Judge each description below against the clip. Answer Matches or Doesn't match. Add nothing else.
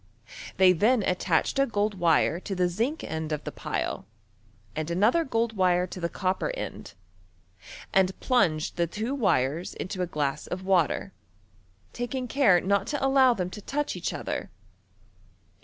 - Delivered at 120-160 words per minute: Matches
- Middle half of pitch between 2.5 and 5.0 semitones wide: Doesn't match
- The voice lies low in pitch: Doesn't match